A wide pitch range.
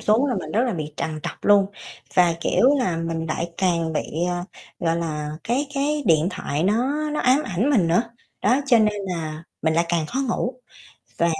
Yes: wide, 7.0 semitones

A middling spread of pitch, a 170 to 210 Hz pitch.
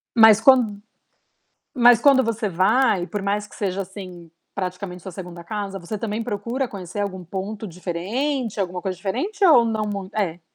Yes: average, 3.6 semitones; high, 205 Hz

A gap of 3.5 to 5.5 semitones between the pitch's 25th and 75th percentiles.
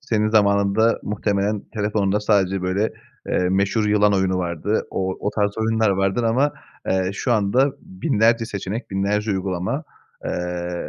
No: narrow, 2.5 semitones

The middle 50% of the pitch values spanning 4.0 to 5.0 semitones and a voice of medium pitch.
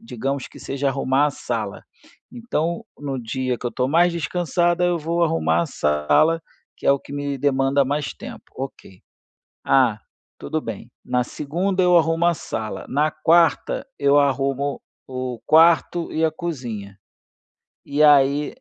Yes: average, 4.3 semitones; medium, 145 Hz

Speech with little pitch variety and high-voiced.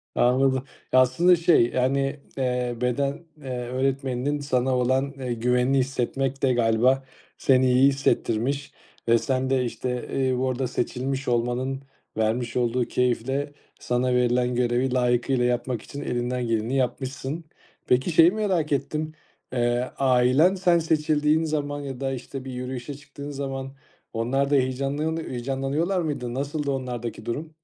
No: narrow, 2.3 semitones; low, 130 Hz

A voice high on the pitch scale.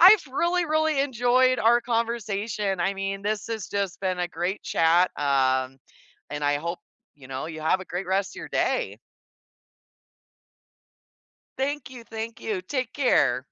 Yes: high, 200 Hz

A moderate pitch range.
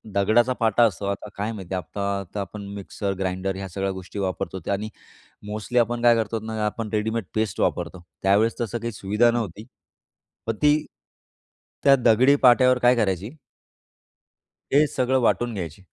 Yes: average, 3.4 semitones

